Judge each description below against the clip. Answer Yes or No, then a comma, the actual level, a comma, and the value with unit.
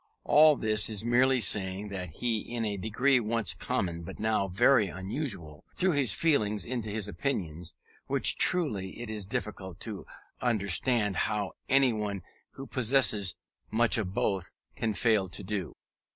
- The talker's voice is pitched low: Yes, low, 105 Hz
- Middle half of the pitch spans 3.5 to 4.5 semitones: Yes, average, 4.0 semitones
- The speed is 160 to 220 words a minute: No, average, 150 wpm